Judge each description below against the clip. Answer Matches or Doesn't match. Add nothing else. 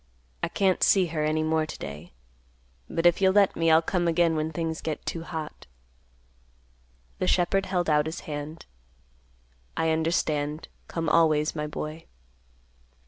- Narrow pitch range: Matches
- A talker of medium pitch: Matches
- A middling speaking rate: Matches